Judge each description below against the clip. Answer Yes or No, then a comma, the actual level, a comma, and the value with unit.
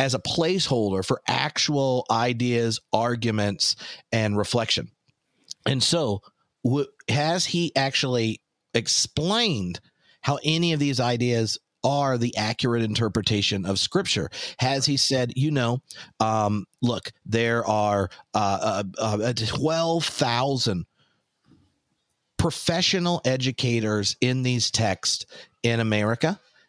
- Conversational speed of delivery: No, slow, 105 wpm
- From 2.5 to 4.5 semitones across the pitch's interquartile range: Yes, average, 3.9 semitones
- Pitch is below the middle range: Yes, low, 120 Hz